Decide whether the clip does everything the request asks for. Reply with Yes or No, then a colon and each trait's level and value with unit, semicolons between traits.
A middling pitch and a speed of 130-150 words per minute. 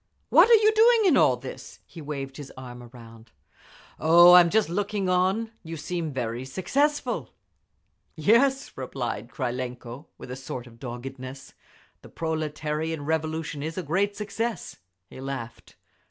Yes: medium, 155 Hz; average, 140 wpm